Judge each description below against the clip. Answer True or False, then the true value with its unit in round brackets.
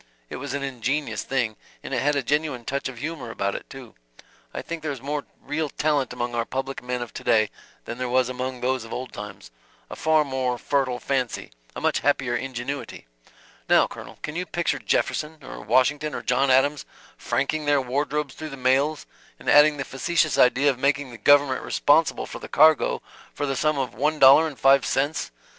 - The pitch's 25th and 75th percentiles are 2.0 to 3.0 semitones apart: True (2.6 semitones)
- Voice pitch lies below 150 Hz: True (135 Hz)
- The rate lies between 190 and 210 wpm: True (200 wpm)